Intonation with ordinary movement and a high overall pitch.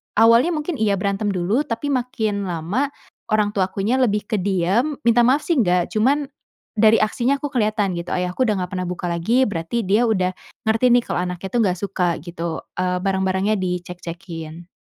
Yes: average, 4.7 semitones; high, 205 Hz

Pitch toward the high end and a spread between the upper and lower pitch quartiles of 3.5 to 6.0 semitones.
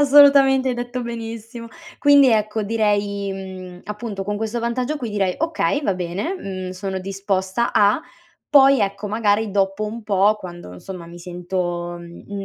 Yes: high, 210 Hz; average, 3.8 semitones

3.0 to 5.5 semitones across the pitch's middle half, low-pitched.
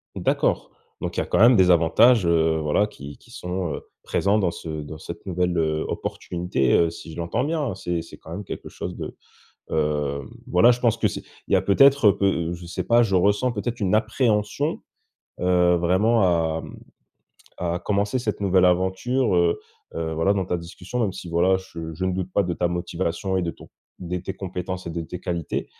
Yes: average, 3.4 semitones; very low, 90 Hz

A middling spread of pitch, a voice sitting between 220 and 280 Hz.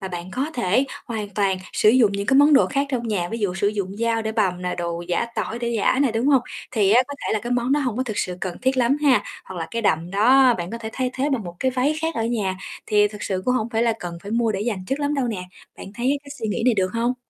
Yes: average, 4.4 semitones; high, 225 Hz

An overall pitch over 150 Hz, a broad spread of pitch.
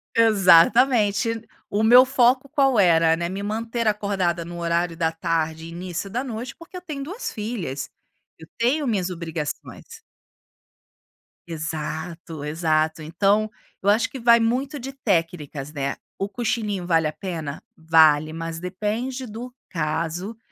Yes: high, 190 Hz; wide, 6.1 semitones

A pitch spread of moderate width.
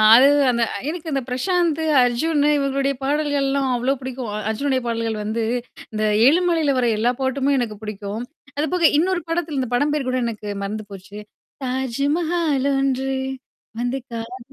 Yes: average, 3.9 semitones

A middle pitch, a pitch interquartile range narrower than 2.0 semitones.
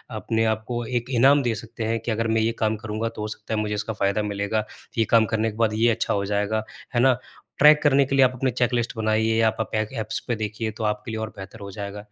No: low, 110 Hz; narrow, 1.6 semitones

